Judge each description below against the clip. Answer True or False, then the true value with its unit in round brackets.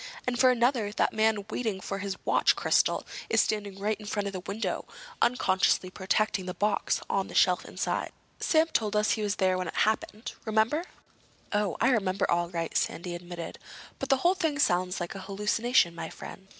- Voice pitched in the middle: False (205 Hz)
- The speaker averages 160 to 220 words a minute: True (190 wpm)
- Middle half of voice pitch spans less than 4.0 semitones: True (3.1 semitones)